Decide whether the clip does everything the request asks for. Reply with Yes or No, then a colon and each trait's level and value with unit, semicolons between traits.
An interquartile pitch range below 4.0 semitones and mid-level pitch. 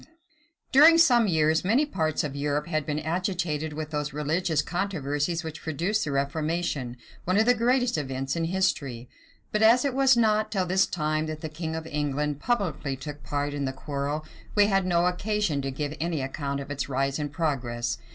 No: average, 4.7 semitones; medium, 155 Hz